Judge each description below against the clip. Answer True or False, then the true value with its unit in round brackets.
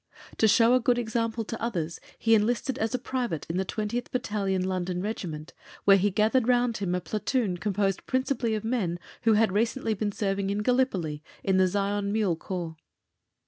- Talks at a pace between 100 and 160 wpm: False (185 wpm)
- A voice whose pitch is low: False (210 Hz)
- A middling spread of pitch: True (3.6 semitones)